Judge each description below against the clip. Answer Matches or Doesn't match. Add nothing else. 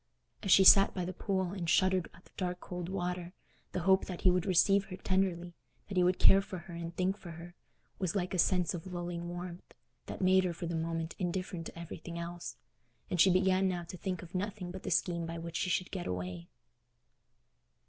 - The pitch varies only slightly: Matches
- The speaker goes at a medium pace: Doesn't match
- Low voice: Doesn't match